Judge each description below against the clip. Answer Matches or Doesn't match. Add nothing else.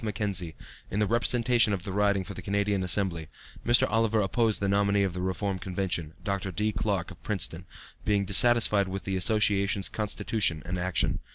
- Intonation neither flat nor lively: Doesn't match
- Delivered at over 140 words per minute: Matches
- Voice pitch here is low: Matches